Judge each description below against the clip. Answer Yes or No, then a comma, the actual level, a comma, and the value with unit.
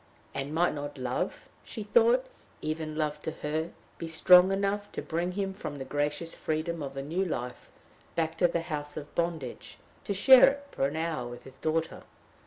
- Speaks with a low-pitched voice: No, medium, 160 Hz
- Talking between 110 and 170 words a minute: No, average, 190 wpm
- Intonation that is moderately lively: Yes, average, 3.4 semitones